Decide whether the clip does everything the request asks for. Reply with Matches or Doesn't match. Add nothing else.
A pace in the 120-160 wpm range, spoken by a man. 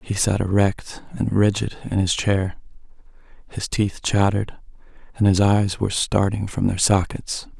Matches